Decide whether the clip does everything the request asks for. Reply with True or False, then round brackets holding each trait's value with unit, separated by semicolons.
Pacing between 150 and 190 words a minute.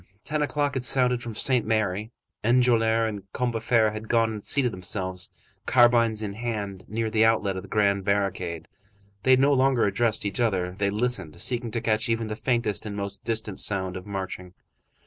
True (180 wpm)